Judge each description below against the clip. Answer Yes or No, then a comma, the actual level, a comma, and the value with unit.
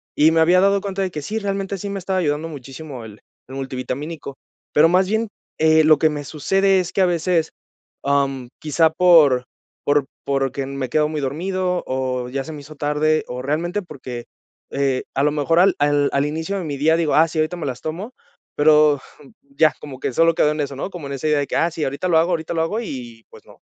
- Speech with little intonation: No, average, 3.8 semitones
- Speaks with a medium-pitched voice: Yes, medium, 155 Hz